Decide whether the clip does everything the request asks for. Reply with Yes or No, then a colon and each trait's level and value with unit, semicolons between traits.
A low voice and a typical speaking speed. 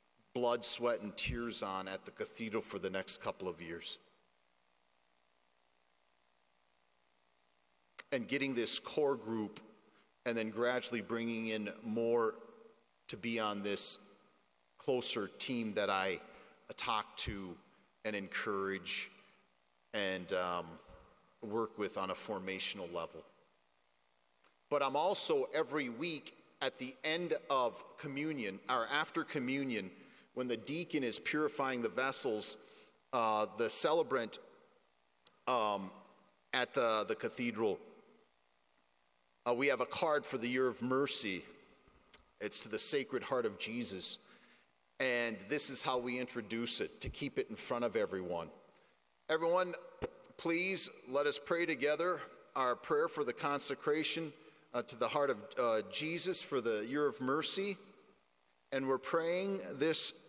No: low, 115 Hz; slow, 130 wpm